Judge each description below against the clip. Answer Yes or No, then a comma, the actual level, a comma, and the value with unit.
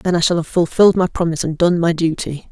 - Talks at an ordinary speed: No, fast, 265 wpm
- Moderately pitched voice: Yes, medium, 170 Hz